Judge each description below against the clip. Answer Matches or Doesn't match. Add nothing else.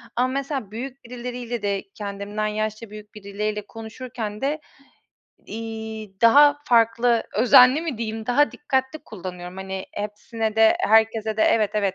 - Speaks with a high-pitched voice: Matches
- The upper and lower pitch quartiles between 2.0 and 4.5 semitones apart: Matches